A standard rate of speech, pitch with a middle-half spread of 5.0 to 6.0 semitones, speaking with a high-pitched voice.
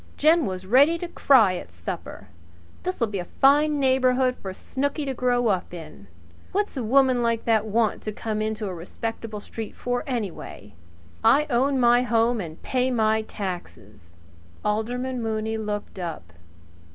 No: average, 160 wpm; average, 4.6 semitones; high, 225 Hz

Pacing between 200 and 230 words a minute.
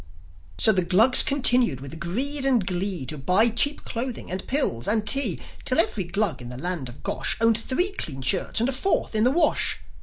Yes: fast, 205 wpm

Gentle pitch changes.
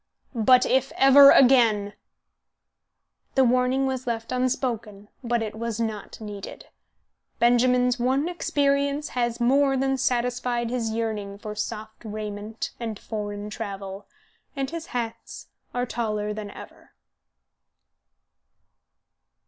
No: average, 3.2 semitones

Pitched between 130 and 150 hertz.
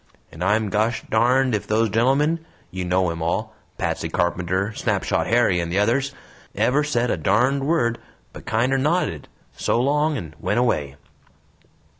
No: low, 115 Hz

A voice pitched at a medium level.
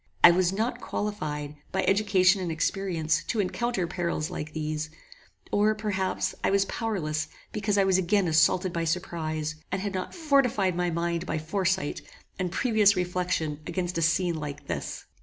Yes: medium, 180 Hz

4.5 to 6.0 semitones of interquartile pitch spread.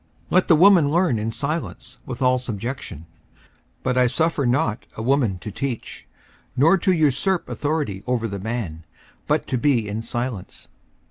Yes: average, 5.2 semitones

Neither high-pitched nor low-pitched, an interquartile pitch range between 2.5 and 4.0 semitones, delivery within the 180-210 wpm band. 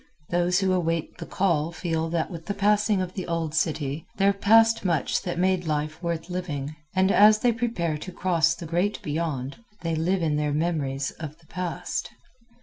Yes: medium, 170 Hz; average, 3.1 semitones; average, 190 wpm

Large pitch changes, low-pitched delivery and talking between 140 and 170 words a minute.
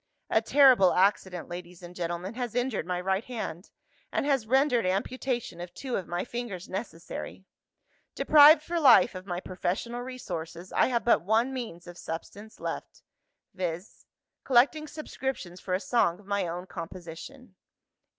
No: wide, 5.9 semitones; high, 200 Hz; average, 150 wpm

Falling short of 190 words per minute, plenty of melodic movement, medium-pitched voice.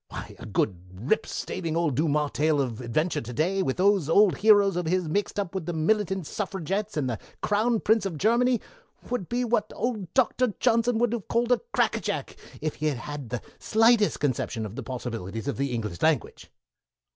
No: average, 200 wpm; wide, 7.5 semitones; medium, 175 Hz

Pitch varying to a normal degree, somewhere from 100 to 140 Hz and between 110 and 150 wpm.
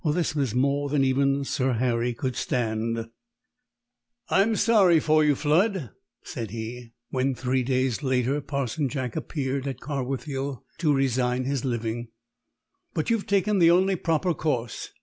Yes: average, 3.8 semitones; low, 135 Hz; average, 145 wpm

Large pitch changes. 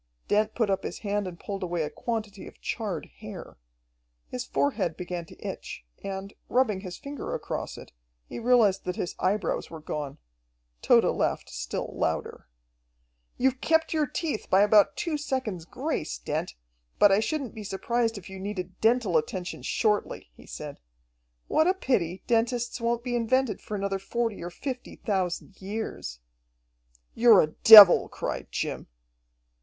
No: average, 4.6 semitones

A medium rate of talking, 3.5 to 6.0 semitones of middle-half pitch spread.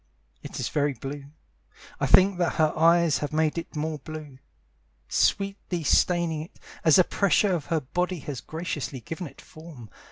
No: average, 165 wpm; average, 3.0 semitones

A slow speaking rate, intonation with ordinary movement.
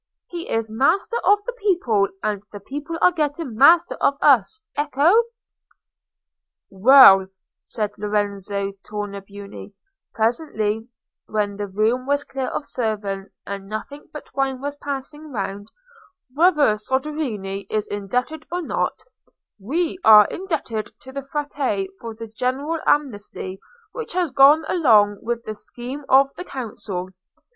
No: slow, 130 wpm; wide, 6.2 semitones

